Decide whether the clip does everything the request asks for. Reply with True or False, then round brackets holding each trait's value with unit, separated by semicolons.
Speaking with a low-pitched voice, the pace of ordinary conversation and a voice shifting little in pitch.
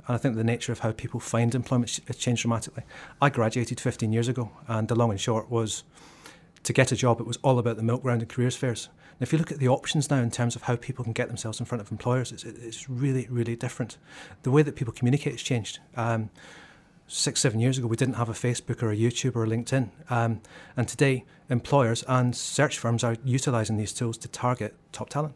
False (120 Hz; 240 wpm; 2.1 semitones)